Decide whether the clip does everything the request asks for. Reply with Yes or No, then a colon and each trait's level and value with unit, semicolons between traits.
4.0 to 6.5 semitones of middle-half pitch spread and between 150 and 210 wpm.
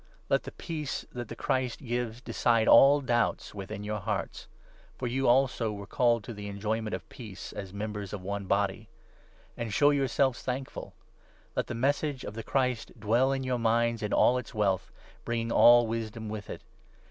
No: average, 3.2 semitones; average, 185 wpm